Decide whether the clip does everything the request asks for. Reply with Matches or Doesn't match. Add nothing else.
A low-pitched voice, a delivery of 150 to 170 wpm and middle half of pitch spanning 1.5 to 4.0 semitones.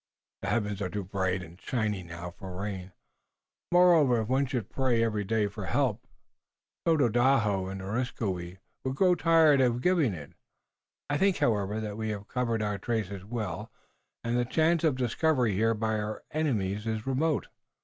Doesn't match